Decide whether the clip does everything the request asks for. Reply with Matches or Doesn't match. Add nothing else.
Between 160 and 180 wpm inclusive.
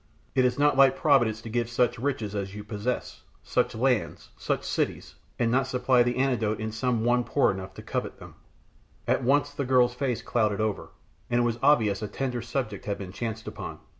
Doesn't match